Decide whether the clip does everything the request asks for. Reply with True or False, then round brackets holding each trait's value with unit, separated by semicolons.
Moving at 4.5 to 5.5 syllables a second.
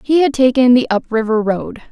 True (5.3 syllables/s)